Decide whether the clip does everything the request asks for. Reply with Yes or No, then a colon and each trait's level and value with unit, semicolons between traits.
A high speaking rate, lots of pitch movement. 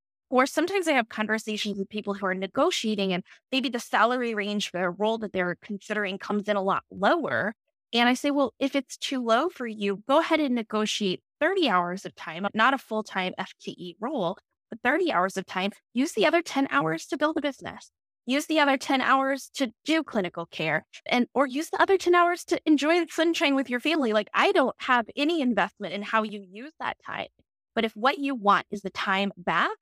Yes: fast, 215 wpm; wide, 6.1 semitones